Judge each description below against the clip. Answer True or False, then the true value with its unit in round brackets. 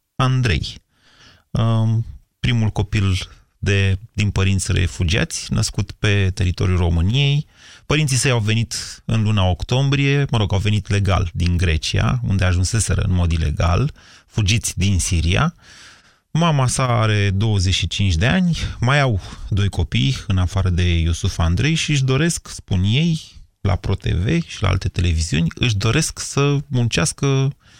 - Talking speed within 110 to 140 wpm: True (135 wpm)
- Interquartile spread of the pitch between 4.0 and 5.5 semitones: True (4.9 semitones)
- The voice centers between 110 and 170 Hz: False (100 Hz)